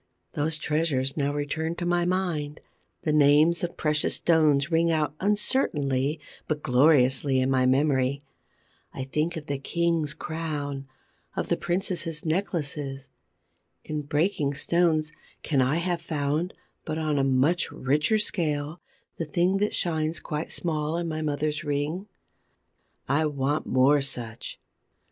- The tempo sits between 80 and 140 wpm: Yes, slow, 135 wpm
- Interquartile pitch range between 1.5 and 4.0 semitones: Yes, average, 2.8 semitones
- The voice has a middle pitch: Yes, medium, 150 Hz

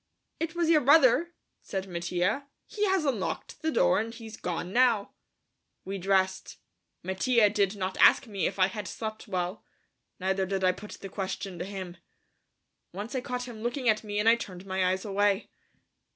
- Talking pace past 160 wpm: Yes, average, 180 wpm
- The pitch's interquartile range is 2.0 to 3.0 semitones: No, average, 4.3 semitones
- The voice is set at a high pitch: Yes, high, 205 Hz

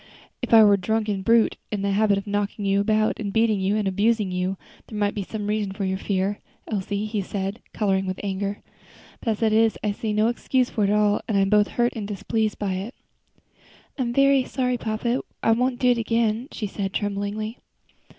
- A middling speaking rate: No, fast, 215 wpm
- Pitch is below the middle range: No, high, 210 Hz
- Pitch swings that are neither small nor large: No, narrow, 2.1 semitones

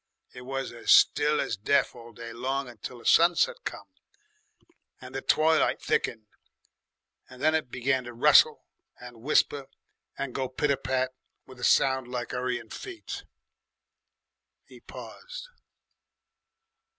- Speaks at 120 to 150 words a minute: Yes, slow, 135 wpm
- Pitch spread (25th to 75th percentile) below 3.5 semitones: Yes, average, 2.9 semitones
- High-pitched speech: No, low, 130 Hz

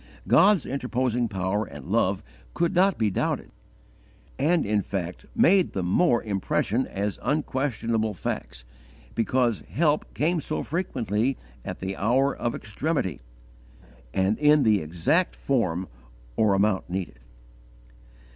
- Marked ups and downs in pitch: Yes, wide, 6.8 semitones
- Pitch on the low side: Yes, low, 115 Hz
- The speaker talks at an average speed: No, slow, 120 wpm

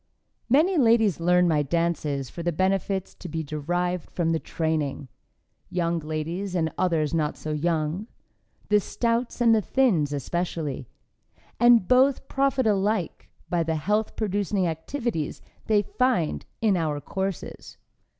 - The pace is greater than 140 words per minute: No, slow, 135 wpm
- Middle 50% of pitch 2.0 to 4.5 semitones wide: No, average, 5.0 semitones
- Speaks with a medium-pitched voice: Yes, medium, 175 Hz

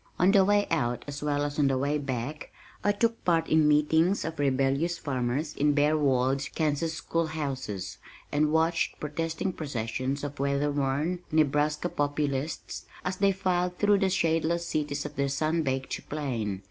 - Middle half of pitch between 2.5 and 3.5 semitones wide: Yes, average, 3.0 semitones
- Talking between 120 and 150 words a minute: No, average, 165 wpm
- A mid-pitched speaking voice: Yes, medium, 150 Hz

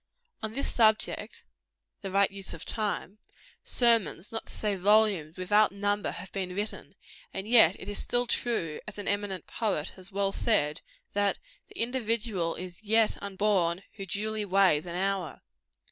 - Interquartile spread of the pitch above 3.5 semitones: No, average, 2.7 semitones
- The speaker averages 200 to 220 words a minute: No, average, 160 wpm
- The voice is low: No, high, 200 Hz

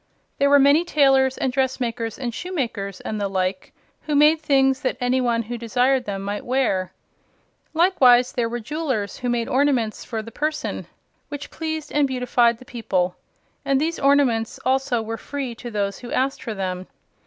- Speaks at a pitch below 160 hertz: No, very high, 250 Hz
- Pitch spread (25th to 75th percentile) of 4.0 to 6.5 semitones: No, average, 3.6 semitones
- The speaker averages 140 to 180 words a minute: Yes, average, 170 wpm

